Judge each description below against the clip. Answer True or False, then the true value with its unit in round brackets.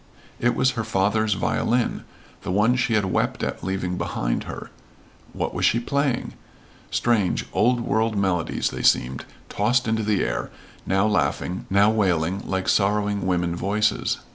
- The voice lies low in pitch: True (105 Hz)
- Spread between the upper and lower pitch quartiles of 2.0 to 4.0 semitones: True (3.2 semitones)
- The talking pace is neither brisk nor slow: True (150 wpm)